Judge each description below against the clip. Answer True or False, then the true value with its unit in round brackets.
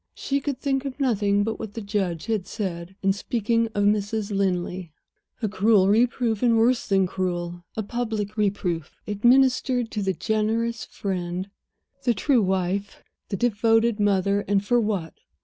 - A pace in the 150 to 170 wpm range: True (155 wpm)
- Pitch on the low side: False (205 Hz)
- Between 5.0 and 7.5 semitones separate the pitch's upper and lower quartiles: False (3.1 semitones)